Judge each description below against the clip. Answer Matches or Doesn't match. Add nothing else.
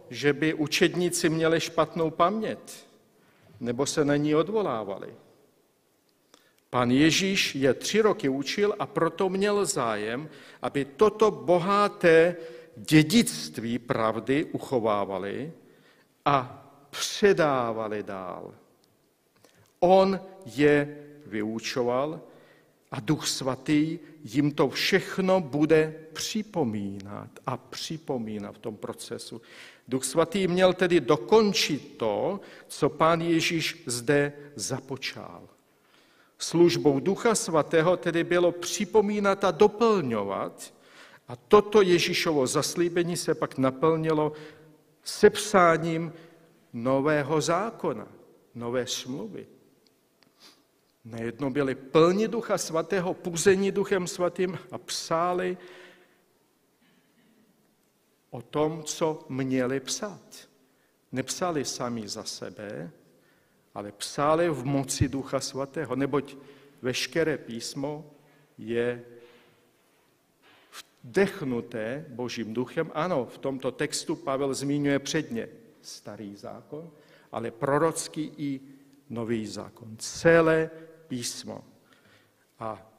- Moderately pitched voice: Matches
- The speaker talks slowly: Matches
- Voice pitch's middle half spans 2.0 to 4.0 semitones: Doesn't match